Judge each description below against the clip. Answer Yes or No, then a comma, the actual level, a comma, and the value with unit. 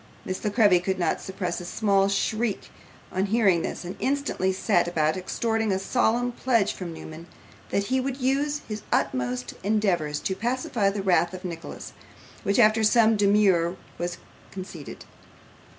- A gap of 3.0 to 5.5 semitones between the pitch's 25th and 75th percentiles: Yes, average, 4.0 semitones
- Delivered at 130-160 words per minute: Yes, average, 155 wpm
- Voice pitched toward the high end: Yes, high, 195 Hz